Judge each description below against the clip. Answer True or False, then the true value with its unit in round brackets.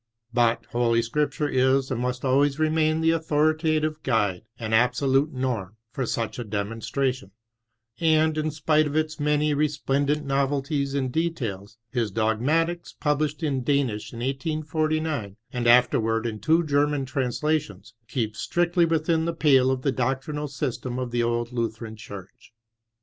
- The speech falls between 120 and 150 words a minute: True (145 wpm)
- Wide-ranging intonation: False (4.5 semitones)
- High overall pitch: False (135 Hz)